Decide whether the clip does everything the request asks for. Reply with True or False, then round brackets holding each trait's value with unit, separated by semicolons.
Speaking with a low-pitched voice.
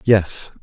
True (100 Hz)